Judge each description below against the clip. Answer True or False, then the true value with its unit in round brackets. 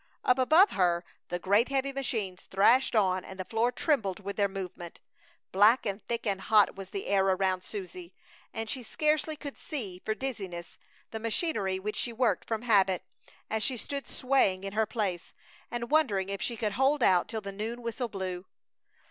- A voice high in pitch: True (210 Hz)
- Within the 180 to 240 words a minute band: True (185 wpm)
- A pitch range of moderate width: True (4.3 semitones)